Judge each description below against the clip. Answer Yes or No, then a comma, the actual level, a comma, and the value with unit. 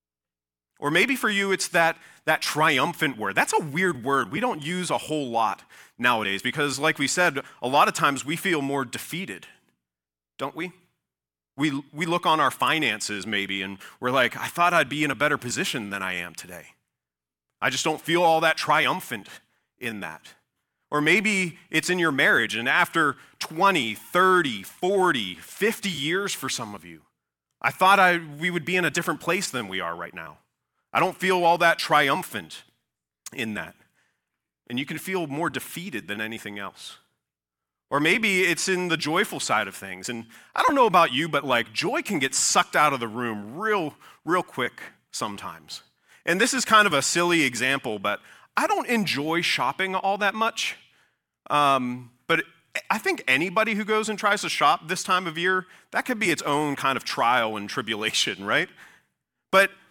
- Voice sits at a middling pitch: Yes, medium, 155 Hz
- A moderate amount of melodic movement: No, wide, 8.2 semitones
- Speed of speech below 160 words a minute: No, average, 185 wpm